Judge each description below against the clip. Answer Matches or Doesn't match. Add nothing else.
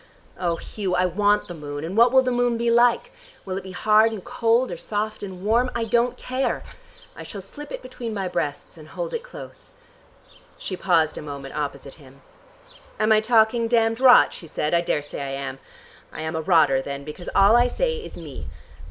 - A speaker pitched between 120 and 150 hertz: Doesn't match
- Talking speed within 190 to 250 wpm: Matches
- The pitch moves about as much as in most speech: Doesn't match